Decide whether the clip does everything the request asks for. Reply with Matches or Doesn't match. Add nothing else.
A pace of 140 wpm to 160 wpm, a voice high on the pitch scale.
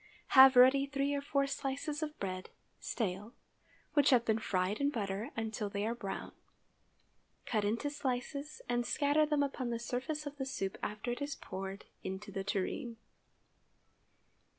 Matches